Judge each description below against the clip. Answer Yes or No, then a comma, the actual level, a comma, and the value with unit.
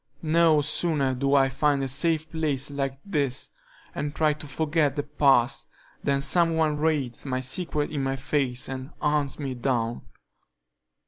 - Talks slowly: No, average, 155 wpm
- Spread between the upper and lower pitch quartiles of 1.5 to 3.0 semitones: Yes, narrow, 2.4 semitones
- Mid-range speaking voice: Yes, medium, 145 Hz